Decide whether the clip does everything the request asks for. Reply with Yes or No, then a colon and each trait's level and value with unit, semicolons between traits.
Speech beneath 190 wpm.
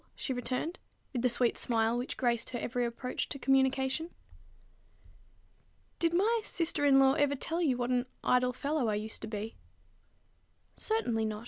Yes: average, 160 wpm